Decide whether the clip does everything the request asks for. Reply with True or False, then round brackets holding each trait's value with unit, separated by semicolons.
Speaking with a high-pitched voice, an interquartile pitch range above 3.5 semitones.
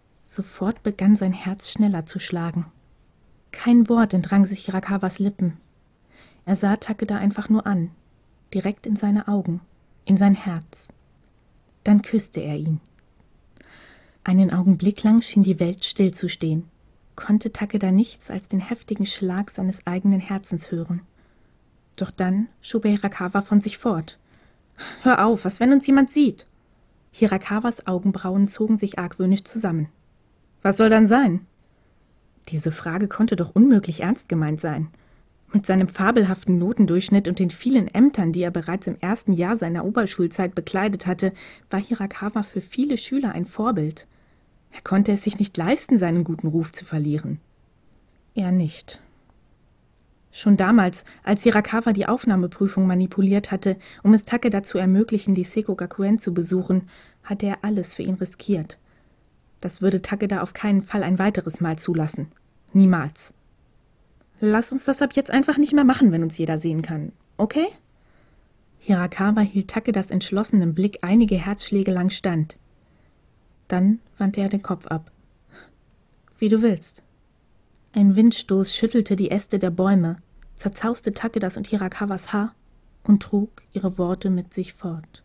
False (195 Hz; 2.9 semitones)